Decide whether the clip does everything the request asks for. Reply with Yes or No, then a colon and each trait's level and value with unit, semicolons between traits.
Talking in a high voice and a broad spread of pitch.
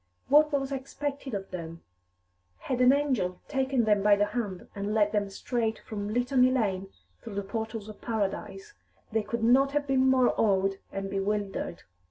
No: high, 220 Hz; average, 4.7 semitones